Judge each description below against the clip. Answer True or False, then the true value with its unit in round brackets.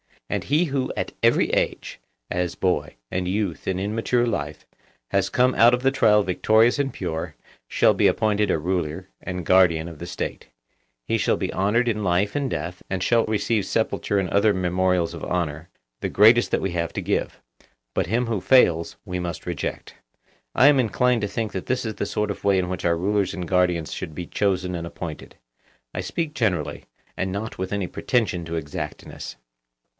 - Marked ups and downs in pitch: False (4.0 semitones)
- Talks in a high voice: False (95 Hz)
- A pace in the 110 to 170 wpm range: False (195 wpm)